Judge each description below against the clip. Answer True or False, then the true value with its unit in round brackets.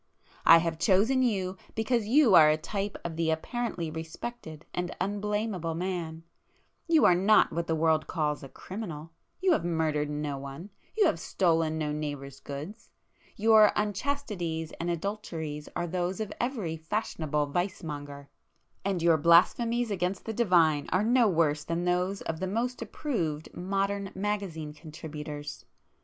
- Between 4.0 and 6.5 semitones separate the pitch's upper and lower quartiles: True (4.7 semitones)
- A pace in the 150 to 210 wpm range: False (140 wpm)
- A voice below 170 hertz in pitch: False (175 Hz)